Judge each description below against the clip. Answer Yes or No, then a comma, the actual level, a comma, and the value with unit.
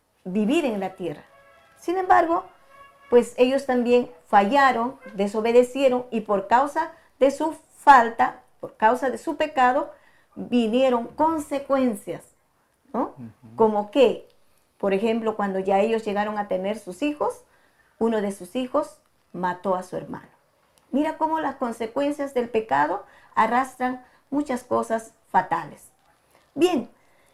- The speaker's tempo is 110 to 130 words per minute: Yes, slow, 125 wpm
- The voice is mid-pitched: No, very high, 250 Hz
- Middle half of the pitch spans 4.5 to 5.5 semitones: Yes, average, 5.0 semitones